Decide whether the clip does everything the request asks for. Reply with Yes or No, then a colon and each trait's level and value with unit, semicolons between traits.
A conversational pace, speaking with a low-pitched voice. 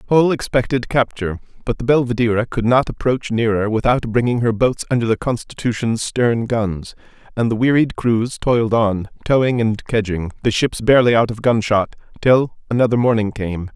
Yes: average, 165 wpm; low, 115 Hz